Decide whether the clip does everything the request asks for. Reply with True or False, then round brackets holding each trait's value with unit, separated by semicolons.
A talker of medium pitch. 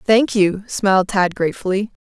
False (200 Hz)